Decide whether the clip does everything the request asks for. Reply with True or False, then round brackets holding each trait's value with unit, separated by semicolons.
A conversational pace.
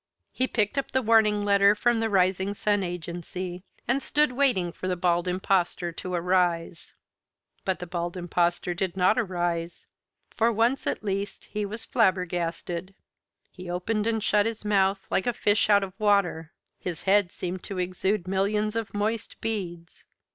True (160 wpm)